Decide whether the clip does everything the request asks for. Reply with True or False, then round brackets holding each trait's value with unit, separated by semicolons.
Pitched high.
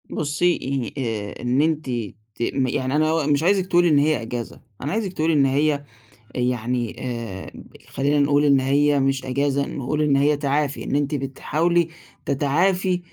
False (145 Hz)